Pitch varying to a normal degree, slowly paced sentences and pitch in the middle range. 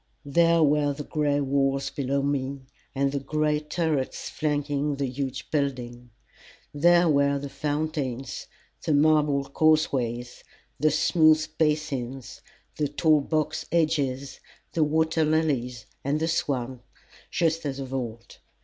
No: narrow, 2.3 semitones; slow, 125 wpm; medium, 145 Hz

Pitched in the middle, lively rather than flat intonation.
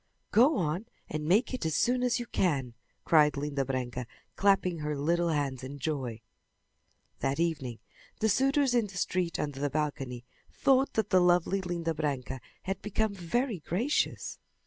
Yes: medium, 170 Hz; wide, 6.2 semitones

